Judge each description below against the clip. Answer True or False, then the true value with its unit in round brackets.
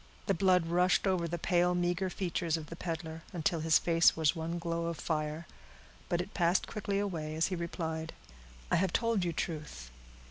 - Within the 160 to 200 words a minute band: True (185 wpm)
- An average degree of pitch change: False (1.9 semitones)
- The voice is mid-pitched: True (170 Hz)